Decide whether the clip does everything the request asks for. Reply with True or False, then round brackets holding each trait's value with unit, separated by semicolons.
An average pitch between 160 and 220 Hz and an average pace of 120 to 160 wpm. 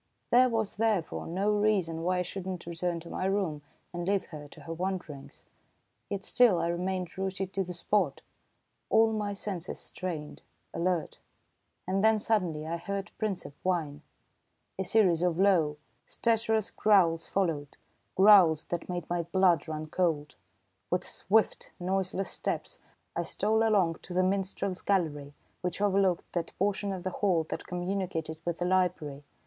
True (185 Hz; 155 wpm)